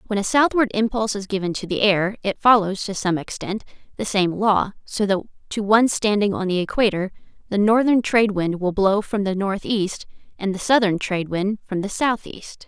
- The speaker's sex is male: No, female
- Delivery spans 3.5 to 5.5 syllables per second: Yes, 5.3 syllables/s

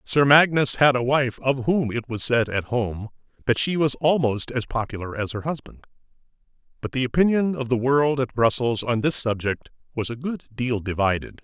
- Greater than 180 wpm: Yes, average, 195 wpm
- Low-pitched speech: Yes, low, 125 Hz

